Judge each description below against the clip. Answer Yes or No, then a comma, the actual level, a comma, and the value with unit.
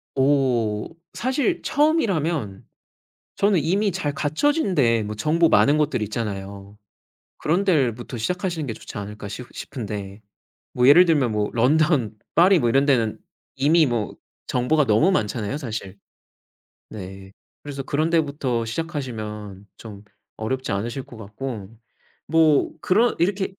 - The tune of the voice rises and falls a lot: Yes, wide, 7.1 semitones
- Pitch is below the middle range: Yes, low, 130 Hz